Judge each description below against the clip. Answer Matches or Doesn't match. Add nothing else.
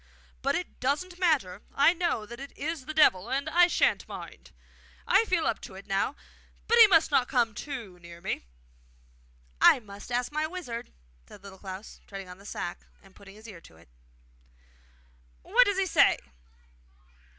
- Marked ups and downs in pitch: Matches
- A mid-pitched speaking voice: Doesn't match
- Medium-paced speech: Matches